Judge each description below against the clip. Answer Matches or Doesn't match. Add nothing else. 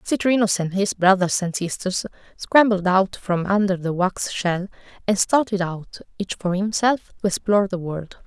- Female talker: Matches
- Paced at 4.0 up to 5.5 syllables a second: Matches